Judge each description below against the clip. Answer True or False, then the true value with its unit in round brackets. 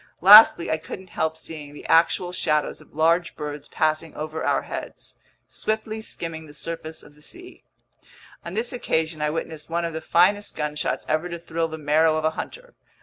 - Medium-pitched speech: True (160 Hz)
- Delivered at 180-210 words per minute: True (185 wpm)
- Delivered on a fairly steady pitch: True (2.2 semitones)